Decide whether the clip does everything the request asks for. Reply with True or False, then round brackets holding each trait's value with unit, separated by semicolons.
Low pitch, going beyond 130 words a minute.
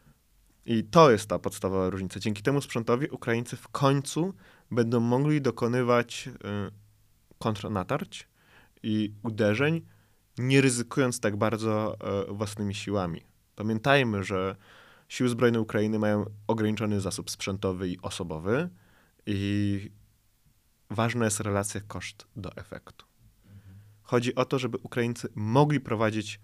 False (110 Hz; 110 wpm)